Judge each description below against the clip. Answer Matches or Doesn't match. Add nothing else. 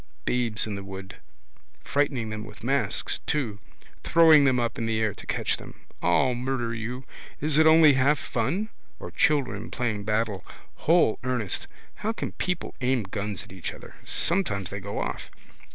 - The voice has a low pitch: Matches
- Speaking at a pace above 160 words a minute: Matches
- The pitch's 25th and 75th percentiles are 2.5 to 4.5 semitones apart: Doesn't match